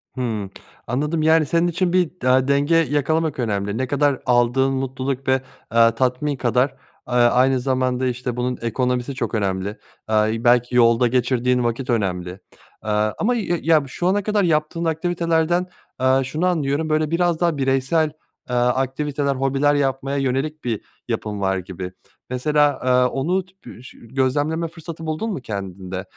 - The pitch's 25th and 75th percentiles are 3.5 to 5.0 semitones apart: Yes, average, 4.1 semitones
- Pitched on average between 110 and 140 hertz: Yes, low, 135 Hz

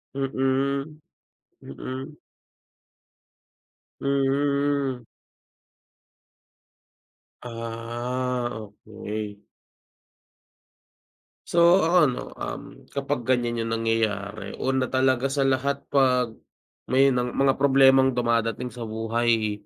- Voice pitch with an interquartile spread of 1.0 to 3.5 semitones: Yes, average, 3.0 semitones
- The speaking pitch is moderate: No, low, 130 Hz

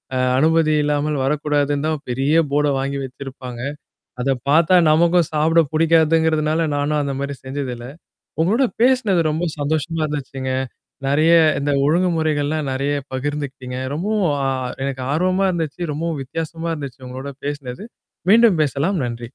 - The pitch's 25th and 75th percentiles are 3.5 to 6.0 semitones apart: No, average, 2.9 semitones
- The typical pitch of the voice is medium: Yes, medium, 150 Hz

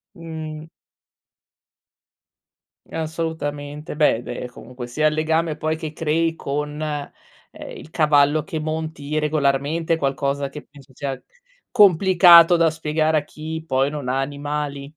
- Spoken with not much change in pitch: Yes, narrow, 2.0 semitones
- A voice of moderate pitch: Yes, medium, 155 Hz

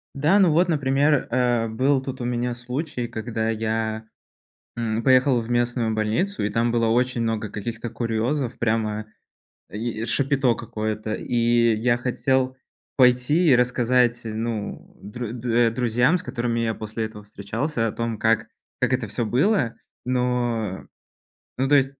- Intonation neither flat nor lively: No, narrow, 2.3 semitones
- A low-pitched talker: Yes, low, 120 Hz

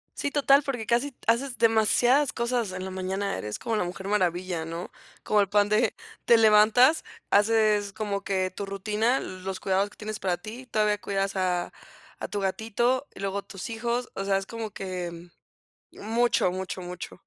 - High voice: Yes, high, 205 Hz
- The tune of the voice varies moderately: Yes, average, 3.4 semitones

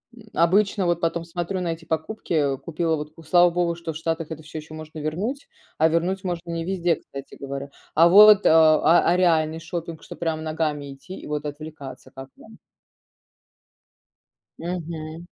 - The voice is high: No, medium, 165 Hz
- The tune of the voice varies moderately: No, narrow, 1.9 semitones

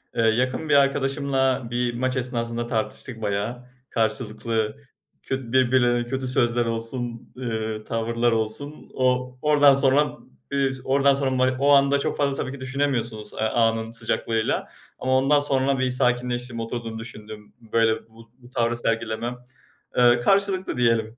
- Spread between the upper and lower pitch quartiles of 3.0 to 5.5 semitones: No, narrow, 2.6 semitones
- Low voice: Yes, low, 120 Hz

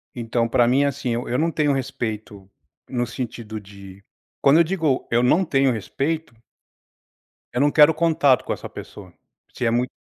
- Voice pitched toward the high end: No, low, 125 Hz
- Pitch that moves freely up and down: No, average, 4.0 semitones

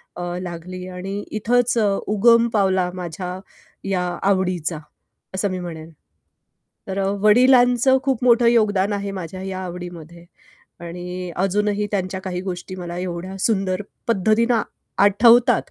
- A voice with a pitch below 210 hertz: Yes, high, 190 Hz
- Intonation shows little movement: No, average, 3.1 semitones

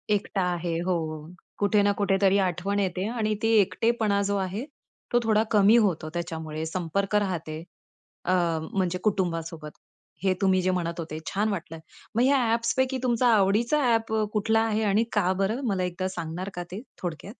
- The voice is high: Yes, high, 195 Hz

